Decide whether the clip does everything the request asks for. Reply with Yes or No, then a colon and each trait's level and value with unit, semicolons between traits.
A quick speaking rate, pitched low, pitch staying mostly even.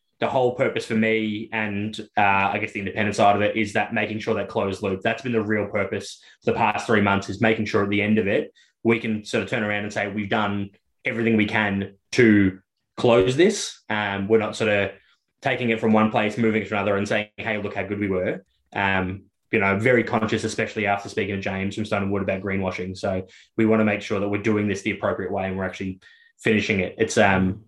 Yes: fast, 240 wpm; low, 105 Hz; narrow, 1.8 semitones